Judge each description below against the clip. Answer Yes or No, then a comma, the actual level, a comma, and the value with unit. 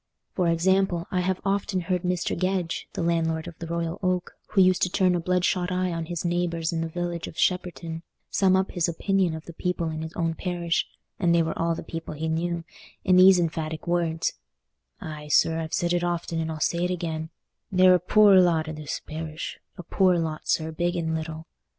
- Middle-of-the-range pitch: Yes, medium, 170 Hz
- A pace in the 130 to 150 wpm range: No, fast, 205 wpm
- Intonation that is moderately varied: No, narrow, 1.9 semitones